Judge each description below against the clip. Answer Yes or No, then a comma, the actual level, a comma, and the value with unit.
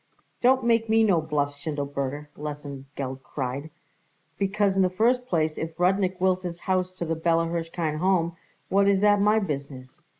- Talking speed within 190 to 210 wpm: No, average, 165 wpm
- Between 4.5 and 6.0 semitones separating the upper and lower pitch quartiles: Yes, average, 4.8 semitones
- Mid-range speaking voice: Yes, medium, 170 Hz